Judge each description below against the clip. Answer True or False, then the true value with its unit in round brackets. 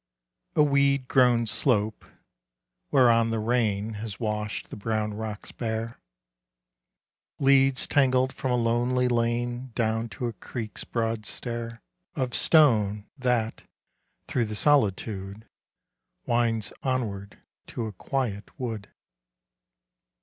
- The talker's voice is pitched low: True (115 Hz)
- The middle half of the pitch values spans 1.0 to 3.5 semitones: True (2.8 semitones)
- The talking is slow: True (110 wpm)